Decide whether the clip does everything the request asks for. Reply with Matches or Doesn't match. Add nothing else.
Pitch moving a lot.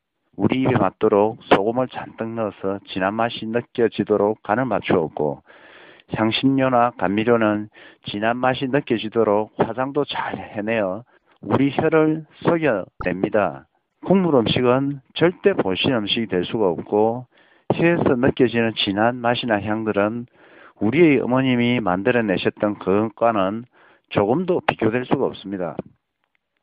Doesn't match